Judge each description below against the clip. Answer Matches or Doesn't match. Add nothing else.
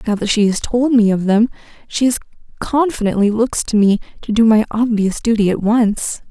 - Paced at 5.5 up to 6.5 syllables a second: Doesn't match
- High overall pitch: Matches